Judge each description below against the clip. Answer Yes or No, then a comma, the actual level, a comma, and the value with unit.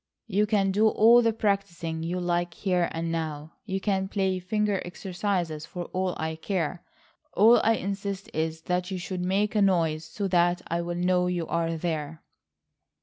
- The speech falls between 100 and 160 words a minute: No, average, 170 wpm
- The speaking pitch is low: No, medium, 180 Hz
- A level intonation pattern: No, average, 3.0 semitones